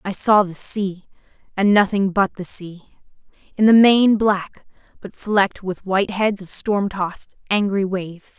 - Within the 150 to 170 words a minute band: Yes, average, 165 wpm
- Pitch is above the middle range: Yes, high, 195 Hz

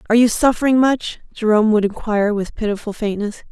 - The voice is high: Yes, high, 220 Hz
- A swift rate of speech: No, average, 170 wpm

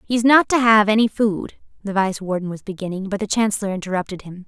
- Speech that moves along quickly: Yes, fast, 215 wpm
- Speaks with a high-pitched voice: Yes, high, 205 Hz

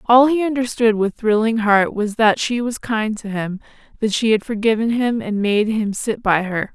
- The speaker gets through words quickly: Yes, fast, 215 wpm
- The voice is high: Yes, high, 220 Hz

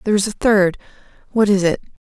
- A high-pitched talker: Yes, high, 200 Hz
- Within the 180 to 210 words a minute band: Yes, fast, 205 wpm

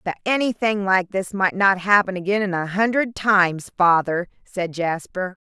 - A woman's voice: Yes, female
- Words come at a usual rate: Yes, average, 165 wpm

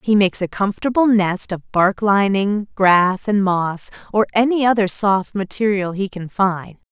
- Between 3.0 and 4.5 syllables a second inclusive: Yes, 4.4 syllables/s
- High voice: Yes, high, 200 Hz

